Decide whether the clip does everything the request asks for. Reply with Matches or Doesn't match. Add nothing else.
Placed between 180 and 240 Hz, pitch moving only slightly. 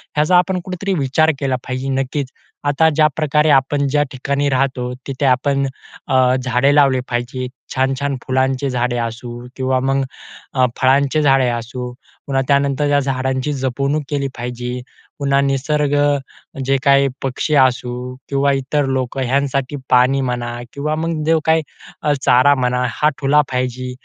Doesn't match